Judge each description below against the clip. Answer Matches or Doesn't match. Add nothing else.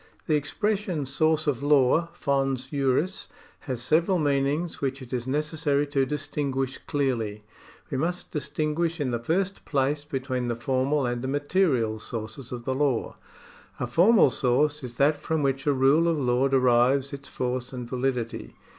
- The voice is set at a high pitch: Doesn't match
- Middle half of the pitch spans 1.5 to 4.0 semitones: Matches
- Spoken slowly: Doesn't match